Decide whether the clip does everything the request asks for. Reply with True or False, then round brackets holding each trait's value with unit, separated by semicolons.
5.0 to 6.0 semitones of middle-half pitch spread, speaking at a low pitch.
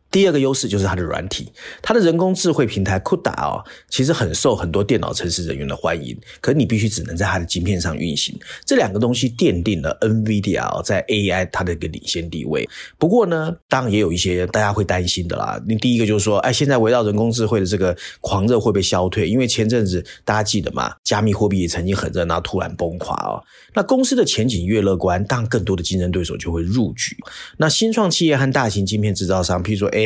True (5.3 semitones; 105 Hz)